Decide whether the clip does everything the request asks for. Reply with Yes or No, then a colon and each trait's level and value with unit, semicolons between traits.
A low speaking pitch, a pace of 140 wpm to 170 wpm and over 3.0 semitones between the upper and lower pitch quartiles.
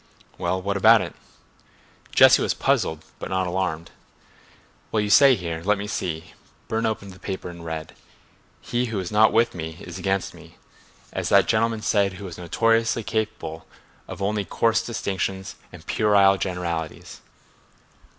Yes: very low, 95 Hz; average, 150 wpm; average, 3.8 semitones